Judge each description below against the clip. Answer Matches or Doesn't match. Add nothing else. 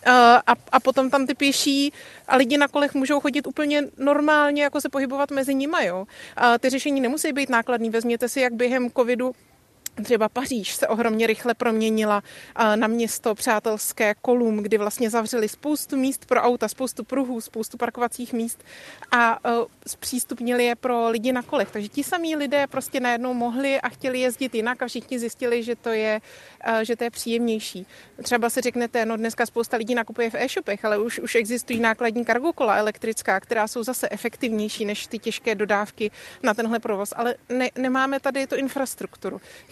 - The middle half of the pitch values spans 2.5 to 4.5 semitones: Matches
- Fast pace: Matches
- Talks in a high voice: Matches